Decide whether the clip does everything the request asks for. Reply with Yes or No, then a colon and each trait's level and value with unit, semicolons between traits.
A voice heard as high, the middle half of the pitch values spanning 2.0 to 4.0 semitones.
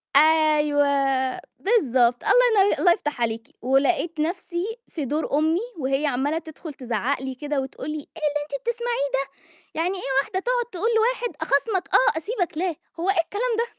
No: very high, 315 Hz; average, 5.3 semitones